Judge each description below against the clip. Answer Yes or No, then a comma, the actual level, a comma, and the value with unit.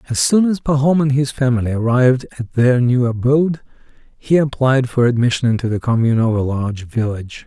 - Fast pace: No, average, 185 wpm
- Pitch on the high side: No, low, 125 Hz